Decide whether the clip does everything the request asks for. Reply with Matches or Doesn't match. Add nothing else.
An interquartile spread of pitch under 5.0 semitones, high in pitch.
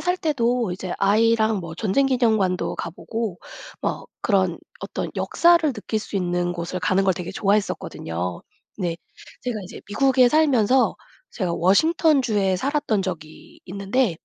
Doesn't match